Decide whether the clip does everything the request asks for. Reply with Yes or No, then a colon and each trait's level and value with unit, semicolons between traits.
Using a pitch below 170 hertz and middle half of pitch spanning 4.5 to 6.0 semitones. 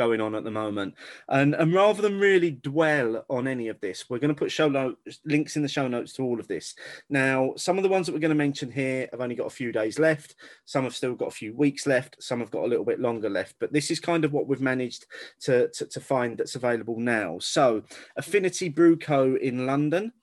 Yes: medium, 140 Hz; average, 4.9 semitones